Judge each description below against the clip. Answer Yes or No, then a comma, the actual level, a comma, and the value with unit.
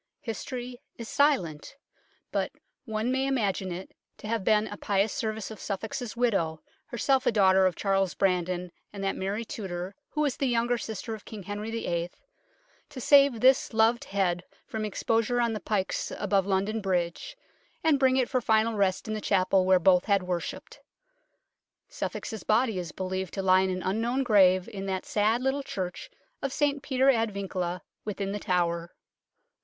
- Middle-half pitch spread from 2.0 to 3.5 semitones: No, average, 4.0 semitones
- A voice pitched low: No, high, 210 Hz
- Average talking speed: Yes, average, 175 wpm